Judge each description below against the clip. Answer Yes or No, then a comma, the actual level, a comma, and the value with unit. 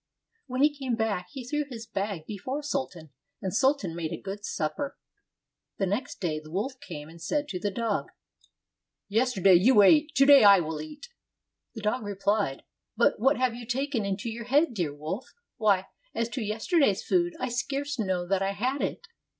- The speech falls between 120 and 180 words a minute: No, average, 190 wpm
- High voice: Yes, high, 220 Hz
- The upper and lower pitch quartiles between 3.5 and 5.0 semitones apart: No, wide, 5.6 semitones